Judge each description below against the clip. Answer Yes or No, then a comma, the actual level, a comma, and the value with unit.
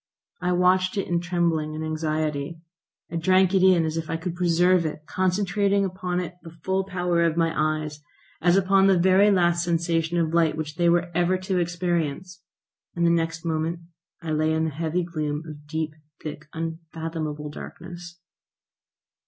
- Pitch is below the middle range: No, medium, 170 Hz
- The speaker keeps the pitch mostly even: Yes, narrow, 2.2 semitones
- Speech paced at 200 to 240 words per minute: No, average, 170 wpm